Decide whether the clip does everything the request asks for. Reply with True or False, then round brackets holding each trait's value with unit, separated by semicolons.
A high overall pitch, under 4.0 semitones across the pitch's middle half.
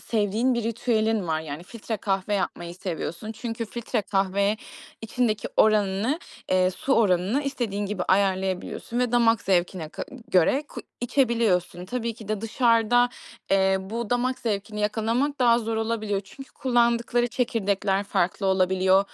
True (215 Hz; 3.6 semitones)